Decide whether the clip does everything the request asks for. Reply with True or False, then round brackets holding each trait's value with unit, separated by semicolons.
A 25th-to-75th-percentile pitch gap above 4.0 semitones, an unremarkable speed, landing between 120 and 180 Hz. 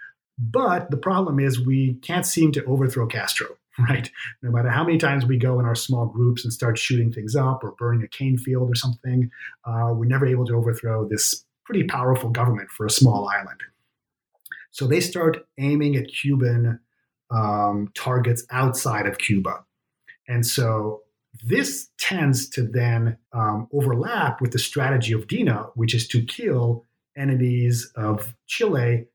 False (2.6 semitones; 165 wpm; 125 Hz)